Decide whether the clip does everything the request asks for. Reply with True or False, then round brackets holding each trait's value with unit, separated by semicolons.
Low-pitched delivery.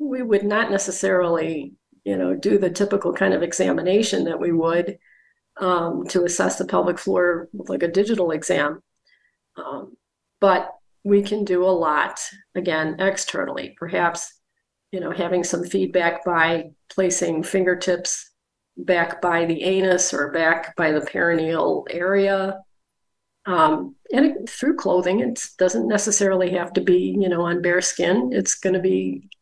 False (180 Hz)